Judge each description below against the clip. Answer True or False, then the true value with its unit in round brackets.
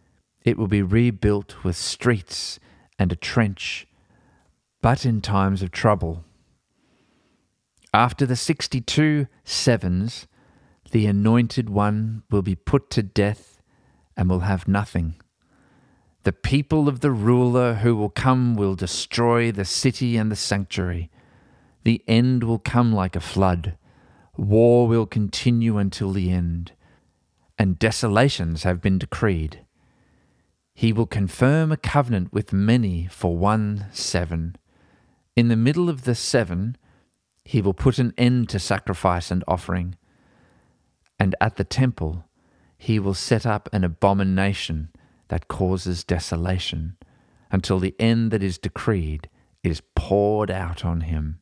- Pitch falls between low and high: False (100 Hz)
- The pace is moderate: False (130 wpm)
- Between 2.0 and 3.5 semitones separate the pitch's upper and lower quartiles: False (4.6 semitones)